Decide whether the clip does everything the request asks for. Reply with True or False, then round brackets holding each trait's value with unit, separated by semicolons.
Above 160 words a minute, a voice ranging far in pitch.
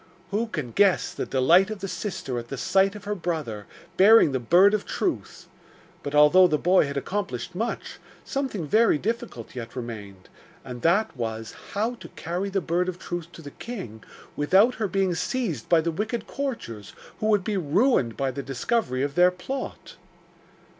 True (180 wpm; 7.3 semitones)